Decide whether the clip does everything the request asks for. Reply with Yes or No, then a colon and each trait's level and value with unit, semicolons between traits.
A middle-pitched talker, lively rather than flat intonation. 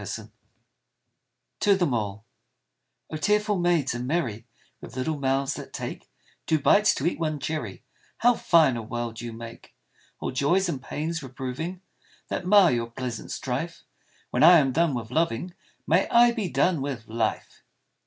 Yes: medium, 145 Hz; wide, 6.2 semitones